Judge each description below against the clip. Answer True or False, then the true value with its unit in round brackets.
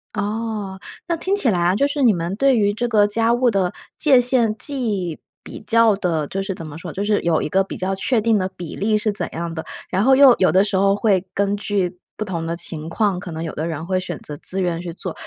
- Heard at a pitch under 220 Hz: True (195 Hz)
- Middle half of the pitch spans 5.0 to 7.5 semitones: False (4.1 semitones)